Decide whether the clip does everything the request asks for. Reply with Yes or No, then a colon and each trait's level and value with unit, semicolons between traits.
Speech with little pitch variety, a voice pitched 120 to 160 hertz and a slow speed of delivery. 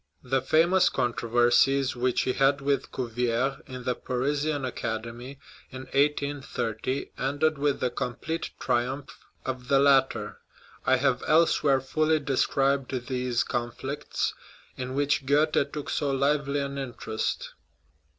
Yes: narrow, 2.3 semitones; low, 135 Hz; slow, 120 wpm